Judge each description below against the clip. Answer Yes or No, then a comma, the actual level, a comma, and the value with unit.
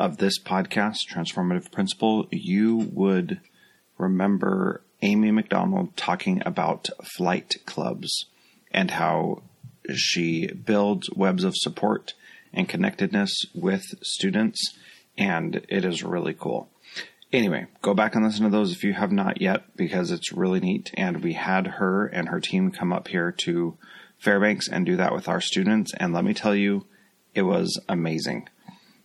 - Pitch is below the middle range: No, medium, 170 Hz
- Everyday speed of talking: Yes, average, 150 wpm